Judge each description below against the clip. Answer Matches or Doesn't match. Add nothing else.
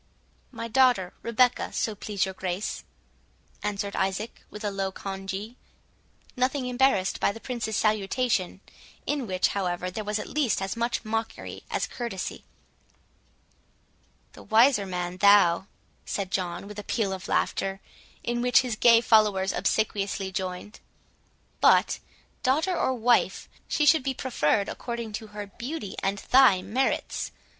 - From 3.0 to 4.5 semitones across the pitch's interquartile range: Matches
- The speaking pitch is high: Matches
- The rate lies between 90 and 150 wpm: Matches